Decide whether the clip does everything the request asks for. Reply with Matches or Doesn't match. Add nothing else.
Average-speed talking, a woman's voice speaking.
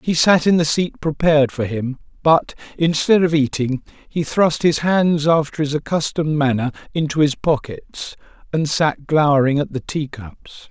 Doesn't match